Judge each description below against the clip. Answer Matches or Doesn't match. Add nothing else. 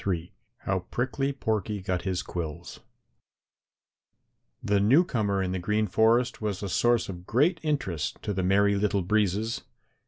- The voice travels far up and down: Doesn't match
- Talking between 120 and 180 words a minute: Matches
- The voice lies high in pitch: Doesn't match